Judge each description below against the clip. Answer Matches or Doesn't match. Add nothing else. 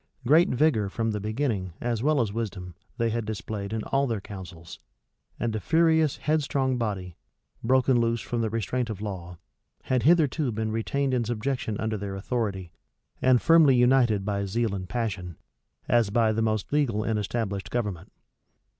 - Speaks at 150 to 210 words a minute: Matches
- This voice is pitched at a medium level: Doesn't match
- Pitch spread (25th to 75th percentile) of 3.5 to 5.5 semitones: Matches